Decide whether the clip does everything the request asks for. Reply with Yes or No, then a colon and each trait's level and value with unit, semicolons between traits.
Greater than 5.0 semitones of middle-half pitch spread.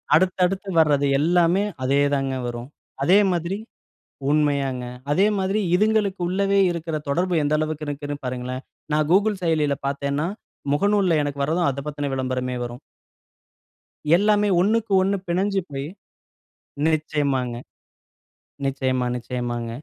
Yes: wide, 5.5 semitones